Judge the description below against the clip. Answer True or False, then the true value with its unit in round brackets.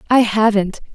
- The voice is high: True (215 Hz)